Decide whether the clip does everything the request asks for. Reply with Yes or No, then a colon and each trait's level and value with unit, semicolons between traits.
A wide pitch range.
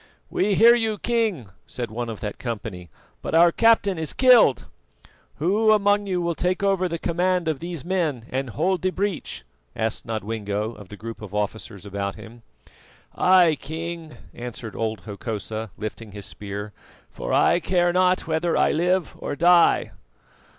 Yes: wide, 8.9 semitones